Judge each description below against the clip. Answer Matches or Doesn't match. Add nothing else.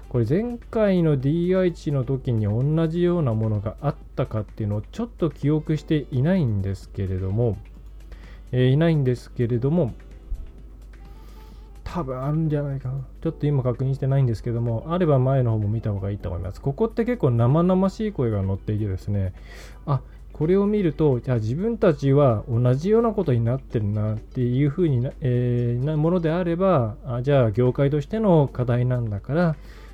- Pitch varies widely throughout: Matches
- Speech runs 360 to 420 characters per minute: Matches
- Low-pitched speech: Matches